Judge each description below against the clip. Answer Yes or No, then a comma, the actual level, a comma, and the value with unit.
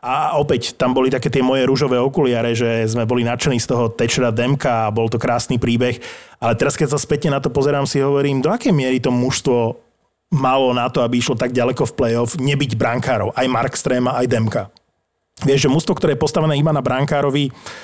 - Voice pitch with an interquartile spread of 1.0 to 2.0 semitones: No, average, 2.7 semitones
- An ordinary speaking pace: No, fast, 210 wpm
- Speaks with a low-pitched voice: Yes, low, 130 Hz